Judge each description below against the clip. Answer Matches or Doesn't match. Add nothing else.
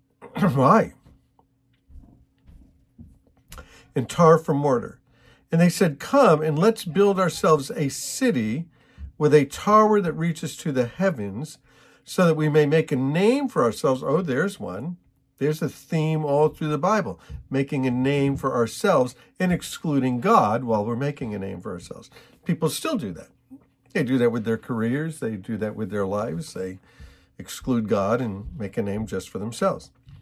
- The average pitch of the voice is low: Doesn't match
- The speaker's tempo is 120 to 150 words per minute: Doesn't match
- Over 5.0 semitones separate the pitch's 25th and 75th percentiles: Matches